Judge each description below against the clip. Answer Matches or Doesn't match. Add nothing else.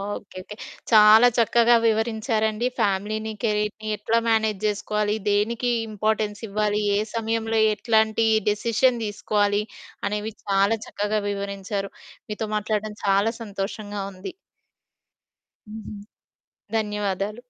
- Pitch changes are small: Matches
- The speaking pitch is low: Doesn't match